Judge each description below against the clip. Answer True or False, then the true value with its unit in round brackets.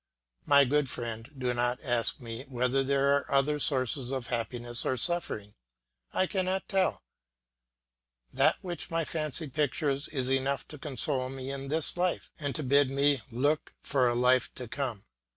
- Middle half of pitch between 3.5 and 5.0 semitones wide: False (2.9 semitones)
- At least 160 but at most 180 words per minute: True (165 wpm)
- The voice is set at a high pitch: False (135 Hz)